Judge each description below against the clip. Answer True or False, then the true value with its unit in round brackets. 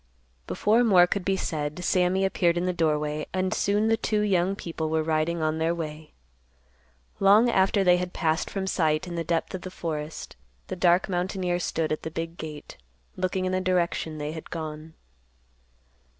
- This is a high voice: False (175 Hz)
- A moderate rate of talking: True (180 wpm)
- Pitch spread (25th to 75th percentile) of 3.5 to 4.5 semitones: False (2.9 semitones)